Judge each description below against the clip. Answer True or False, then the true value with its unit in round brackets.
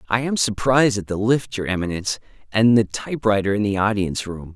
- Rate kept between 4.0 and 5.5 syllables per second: False (6.2 syllables/s)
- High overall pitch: False (105 Hz)